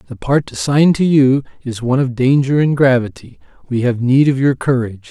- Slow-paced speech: No, average, 200 wpm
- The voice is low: Yes, low, 130 Hz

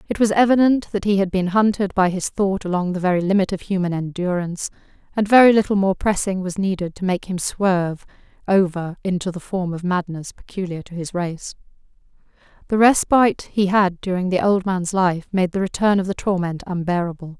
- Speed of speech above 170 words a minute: Yes, average, 190 wpm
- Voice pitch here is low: No, medium, 185 Hz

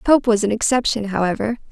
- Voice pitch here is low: No, high, 220 Hz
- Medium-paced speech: Yes, average, 175 wpm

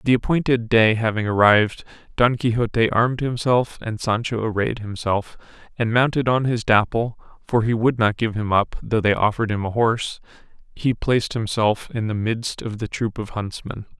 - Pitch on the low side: Yes, low, 115 Hz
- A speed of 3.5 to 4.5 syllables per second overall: Yes, 4.0 syllables/s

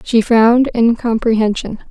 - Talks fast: No, slow, 95 wpm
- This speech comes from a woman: Yes, female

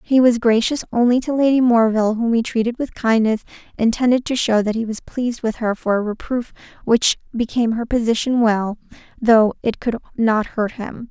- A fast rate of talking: No, average, 190 wpm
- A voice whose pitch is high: Yes, high, 230 Hz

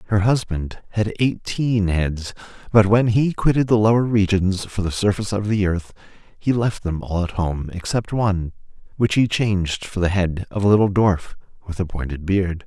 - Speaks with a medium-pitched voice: No, low, 100 Hz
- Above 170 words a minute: Yes, average, 190 wpm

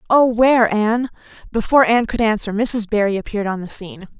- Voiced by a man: No, female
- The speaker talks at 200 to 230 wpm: No, average, 185 wpm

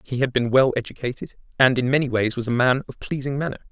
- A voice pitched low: Yes, low, 130 Hz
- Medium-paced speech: No, fast, 240 wpm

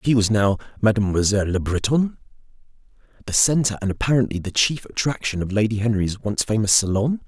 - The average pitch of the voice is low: Yes, low, 110 Hz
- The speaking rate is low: No, average, 155 wpm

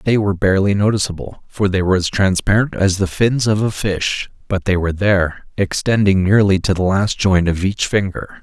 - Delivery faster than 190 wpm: Yes, average, 200 wpm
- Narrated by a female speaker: No, male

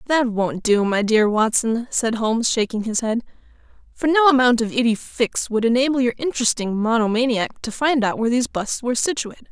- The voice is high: Yes, high, 235 Hz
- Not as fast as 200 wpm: Yes, average, 190 wpm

